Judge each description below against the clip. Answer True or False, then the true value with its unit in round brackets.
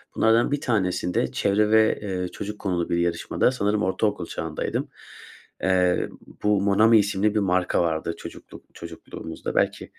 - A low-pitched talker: True (100 Hz)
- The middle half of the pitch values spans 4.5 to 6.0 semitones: False (2.9 semitones)